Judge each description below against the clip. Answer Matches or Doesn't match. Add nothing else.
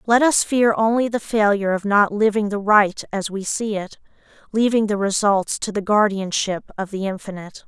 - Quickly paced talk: Doesn't match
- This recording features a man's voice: Doesn't match